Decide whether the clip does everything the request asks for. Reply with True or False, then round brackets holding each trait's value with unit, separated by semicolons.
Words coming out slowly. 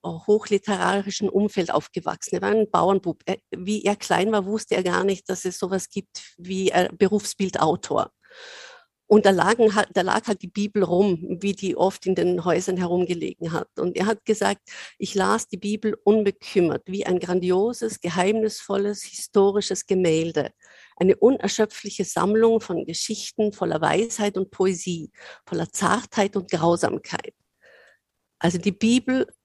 False (145 wpm)